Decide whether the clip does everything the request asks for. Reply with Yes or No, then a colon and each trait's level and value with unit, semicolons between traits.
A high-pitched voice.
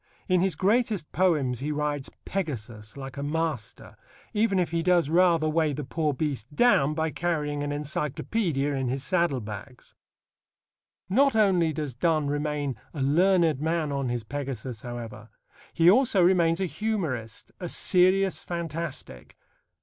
No: medium, 155 Hz